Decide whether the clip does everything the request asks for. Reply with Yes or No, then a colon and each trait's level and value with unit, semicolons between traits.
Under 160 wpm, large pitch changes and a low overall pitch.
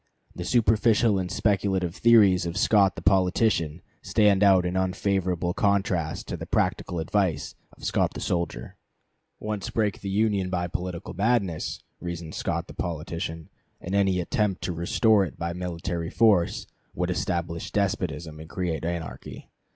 No: average, 145 wpm; average, 2.8 semitones; very low, 90 Hz